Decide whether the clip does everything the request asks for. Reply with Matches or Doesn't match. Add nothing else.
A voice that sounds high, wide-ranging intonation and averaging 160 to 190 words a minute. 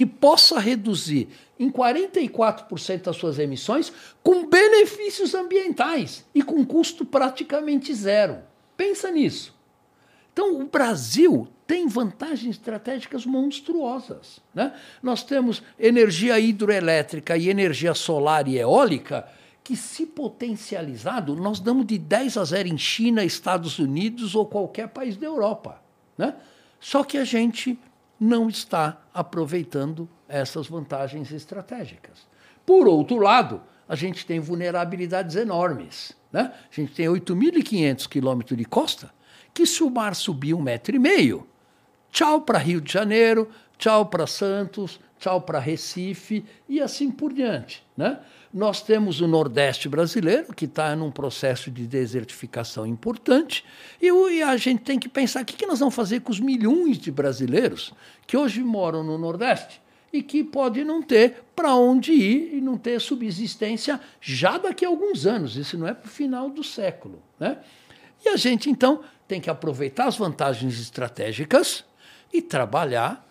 Doesn't match